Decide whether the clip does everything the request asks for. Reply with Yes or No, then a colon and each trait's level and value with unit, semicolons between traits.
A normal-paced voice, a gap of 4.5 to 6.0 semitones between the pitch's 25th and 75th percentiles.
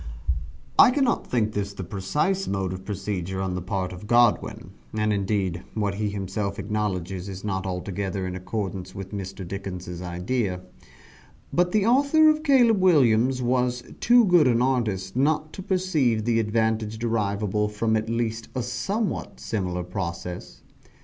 Yes: average, 150 wpm; average, 4.8 semitones